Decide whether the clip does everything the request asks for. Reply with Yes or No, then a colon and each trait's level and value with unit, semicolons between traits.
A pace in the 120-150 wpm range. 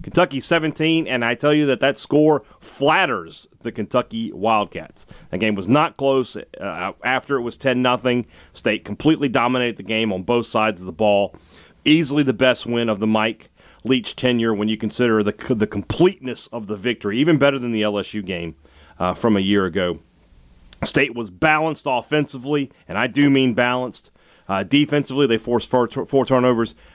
No: average, 180 wpm